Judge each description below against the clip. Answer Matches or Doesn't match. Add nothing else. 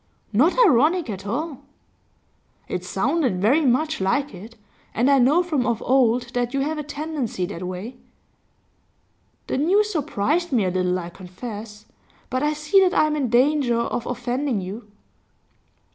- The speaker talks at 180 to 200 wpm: Doesn't match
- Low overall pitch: Doesn't match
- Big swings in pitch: Matches